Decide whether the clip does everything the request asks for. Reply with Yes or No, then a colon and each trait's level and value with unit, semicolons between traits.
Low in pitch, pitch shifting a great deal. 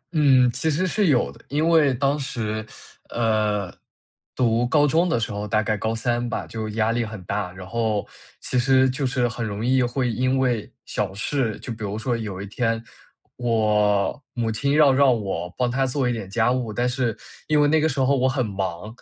No: low, 120 Hz; average, 3.6 semitones